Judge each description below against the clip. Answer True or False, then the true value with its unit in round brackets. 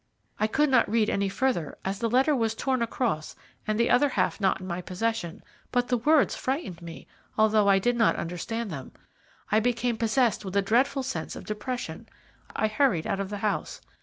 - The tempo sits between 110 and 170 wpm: False (195 wpm)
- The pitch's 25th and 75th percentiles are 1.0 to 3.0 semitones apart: False (3.9 semitones)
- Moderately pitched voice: False (220 Hz)